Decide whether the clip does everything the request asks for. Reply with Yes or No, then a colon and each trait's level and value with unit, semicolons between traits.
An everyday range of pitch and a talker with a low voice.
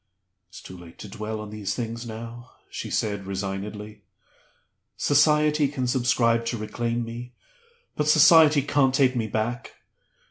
Yes: average, 3.7 semitones; low, 115 Hz